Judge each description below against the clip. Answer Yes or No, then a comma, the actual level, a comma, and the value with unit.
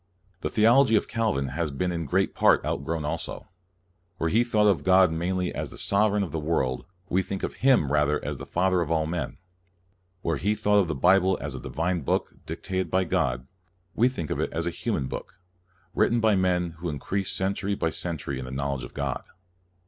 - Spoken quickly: Yes, fast, 210 wpm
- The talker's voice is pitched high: No, very low, 90 Hz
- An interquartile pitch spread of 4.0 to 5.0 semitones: Yes, average, 4.6 semitones